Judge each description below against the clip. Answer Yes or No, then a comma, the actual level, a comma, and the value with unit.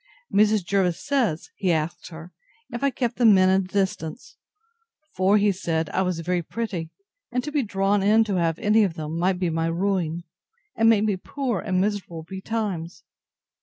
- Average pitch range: Yes, average, 3.8 semitones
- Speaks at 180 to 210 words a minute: Yes, average, 185 wpm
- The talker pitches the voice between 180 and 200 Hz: Yes, high, 190 Hz